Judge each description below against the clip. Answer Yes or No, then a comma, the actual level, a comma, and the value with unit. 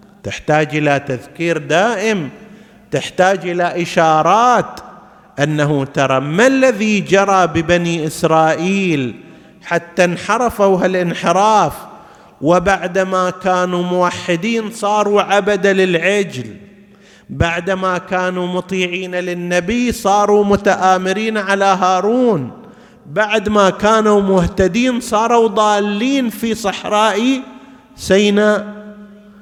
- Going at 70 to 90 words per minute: Yes, average, 80 wpm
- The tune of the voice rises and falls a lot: No, average, 3.1 semitones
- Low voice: No, high, 195 Hz